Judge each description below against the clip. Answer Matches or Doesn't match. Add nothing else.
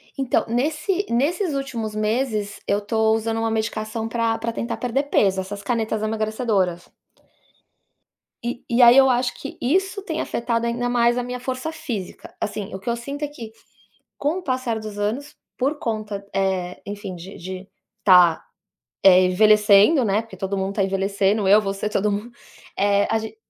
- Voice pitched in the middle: Doesn't match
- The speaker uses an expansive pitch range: Doesn't match